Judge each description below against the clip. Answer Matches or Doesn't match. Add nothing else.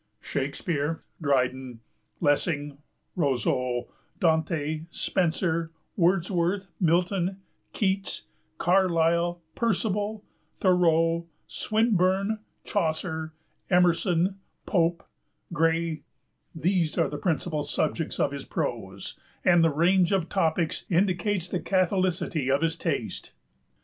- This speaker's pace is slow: Matches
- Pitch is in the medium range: Matches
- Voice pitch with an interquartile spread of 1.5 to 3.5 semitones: Matches